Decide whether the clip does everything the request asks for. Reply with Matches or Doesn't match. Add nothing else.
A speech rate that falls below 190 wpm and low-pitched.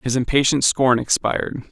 Matches